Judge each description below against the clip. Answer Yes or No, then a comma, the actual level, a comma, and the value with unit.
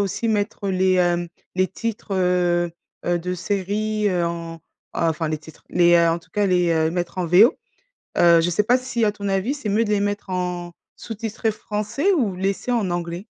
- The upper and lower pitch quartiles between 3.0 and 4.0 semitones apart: Yes, average, 3.3 semitones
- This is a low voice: No, medium, 185 Hz